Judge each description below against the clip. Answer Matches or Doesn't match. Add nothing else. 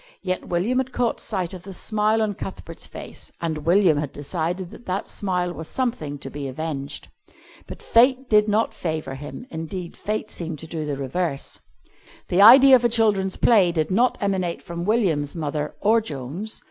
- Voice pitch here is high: Doesn't match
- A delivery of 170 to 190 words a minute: Matches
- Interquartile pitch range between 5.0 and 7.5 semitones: Matches